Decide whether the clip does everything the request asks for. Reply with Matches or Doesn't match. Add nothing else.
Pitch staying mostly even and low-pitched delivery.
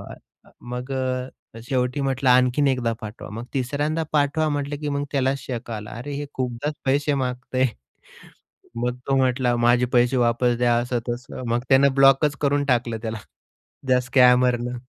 Matches